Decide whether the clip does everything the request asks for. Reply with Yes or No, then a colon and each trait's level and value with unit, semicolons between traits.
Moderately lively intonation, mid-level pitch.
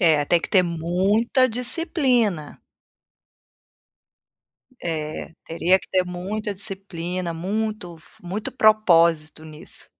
Yes: average, 4.4 semitones; medium, 180 Hz